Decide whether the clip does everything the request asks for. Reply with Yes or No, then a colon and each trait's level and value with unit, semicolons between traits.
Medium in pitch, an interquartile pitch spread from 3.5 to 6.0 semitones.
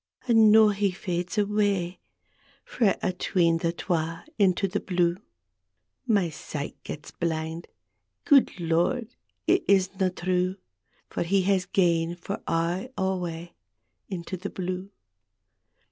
No: medium, 180 Hz; average, 2.7 semitones